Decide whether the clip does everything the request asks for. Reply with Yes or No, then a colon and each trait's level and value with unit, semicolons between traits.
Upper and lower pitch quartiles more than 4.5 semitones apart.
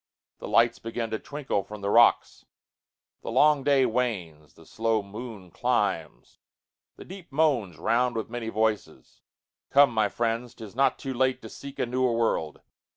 No: average, 3.2 semitones